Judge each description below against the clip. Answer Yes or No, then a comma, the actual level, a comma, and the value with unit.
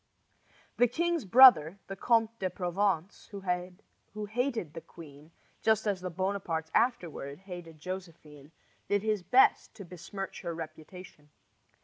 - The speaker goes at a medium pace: No, slow, 125 wpm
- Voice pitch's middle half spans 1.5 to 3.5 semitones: No, average, 4.3 semitones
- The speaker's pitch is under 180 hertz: No, medium, 185 Hz